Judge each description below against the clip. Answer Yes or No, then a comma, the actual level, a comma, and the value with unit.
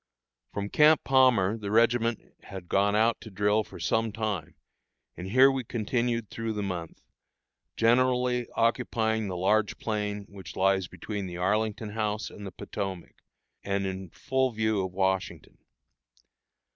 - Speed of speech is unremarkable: Yes, average, 145 wpm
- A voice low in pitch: Yes, low, 105 Hz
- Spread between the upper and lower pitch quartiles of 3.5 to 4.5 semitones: No, average, 3.1 semitones